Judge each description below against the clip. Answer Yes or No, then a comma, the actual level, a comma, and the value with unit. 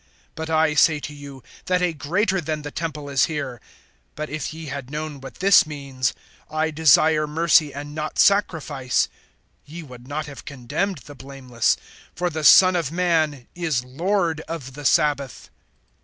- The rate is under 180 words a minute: Yes, average, 165 wpm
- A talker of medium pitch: Yes, medium, 150 Hz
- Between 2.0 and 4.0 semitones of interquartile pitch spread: Yes, average, 2.7 semitones